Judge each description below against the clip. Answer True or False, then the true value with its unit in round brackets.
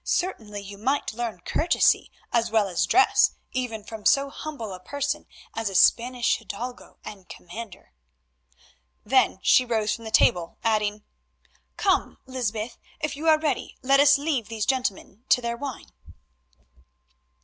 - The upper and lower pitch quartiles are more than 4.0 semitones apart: True (4.7 semitones)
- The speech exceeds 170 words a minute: False (140 wpm)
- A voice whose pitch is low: False (235 Hz)